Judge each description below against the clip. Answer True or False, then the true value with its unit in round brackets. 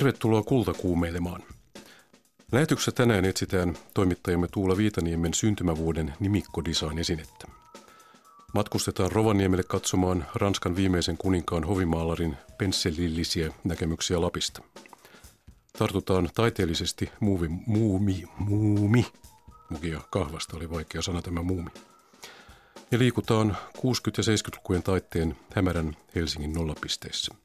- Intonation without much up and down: False (3.8 semitones)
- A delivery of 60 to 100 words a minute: True (95 wpm)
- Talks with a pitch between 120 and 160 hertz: False (90 Hz)